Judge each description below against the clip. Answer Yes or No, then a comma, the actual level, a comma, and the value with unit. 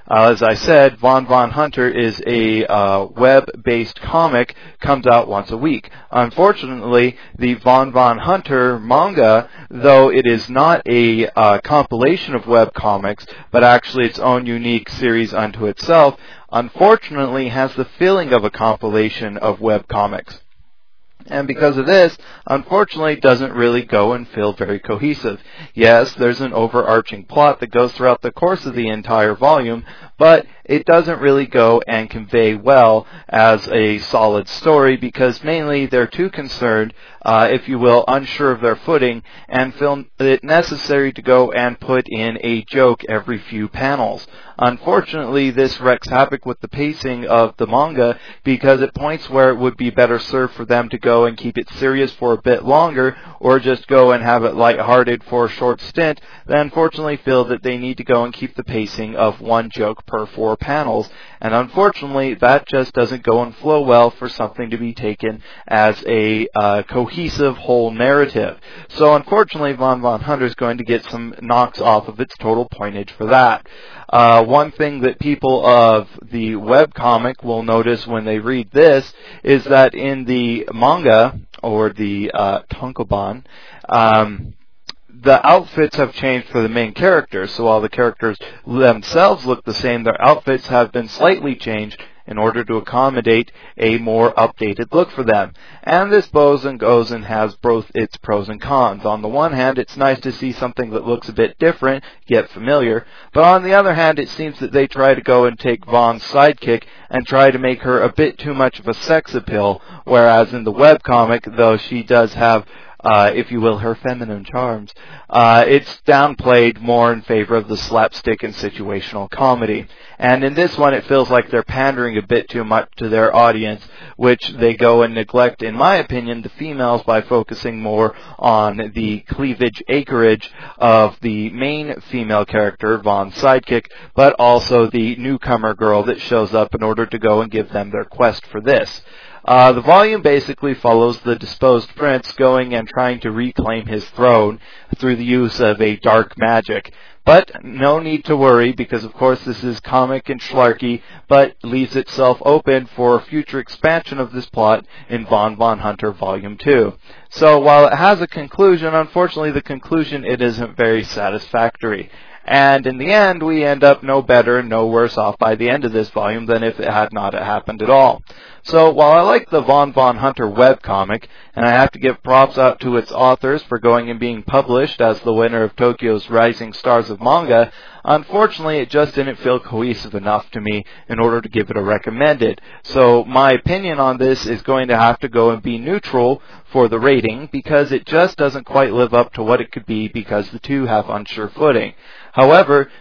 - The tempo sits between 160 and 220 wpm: Yes, average, 185 wpm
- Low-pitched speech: Yes, low, 120 Hz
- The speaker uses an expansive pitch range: No, average, 3.2 semitones